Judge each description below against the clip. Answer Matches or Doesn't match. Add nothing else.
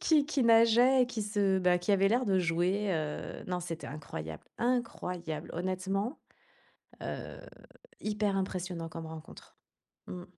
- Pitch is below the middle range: Doesn't match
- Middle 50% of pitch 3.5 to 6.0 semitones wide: Matches